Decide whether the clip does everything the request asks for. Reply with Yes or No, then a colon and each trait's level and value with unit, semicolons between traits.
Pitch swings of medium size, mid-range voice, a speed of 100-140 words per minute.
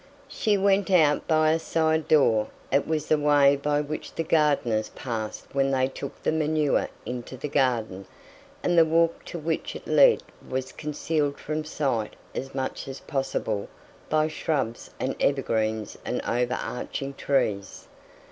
No: average, 3.6 semitones; medium, 145 Hz; average, 155 wpm